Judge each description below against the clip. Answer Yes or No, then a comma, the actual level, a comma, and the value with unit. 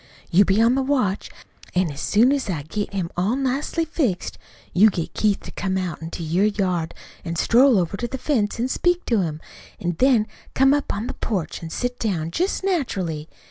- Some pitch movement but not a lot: No, wide, 6.8 semitones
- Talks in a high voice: Yes, high, 205 Hz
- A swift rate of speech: Yes, fast, 210 wpm